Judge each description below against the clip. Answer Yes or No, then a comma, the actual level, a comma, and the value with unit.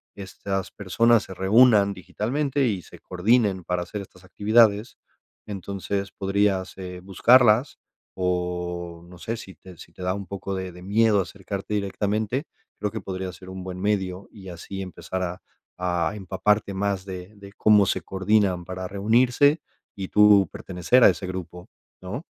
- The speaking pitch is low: Yes, very low, 95 Hz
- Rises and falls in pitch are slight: Yes, narrow, 2.3 semitones